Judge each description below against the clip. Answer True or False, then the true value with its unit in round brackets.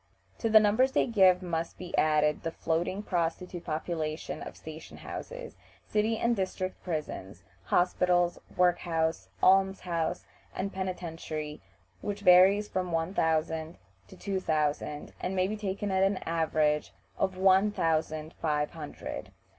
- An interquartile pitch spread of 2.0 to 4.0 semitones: True (3.2 semitones)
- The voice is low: False (180 Hz)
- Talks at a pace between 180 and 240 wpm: False (140 wpm)